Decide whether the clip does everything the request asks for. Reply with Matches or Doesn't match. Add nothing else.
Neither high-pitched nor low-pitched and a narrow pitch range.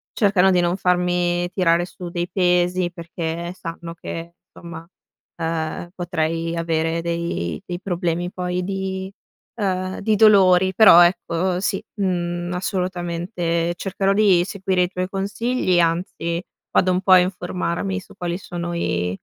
Matches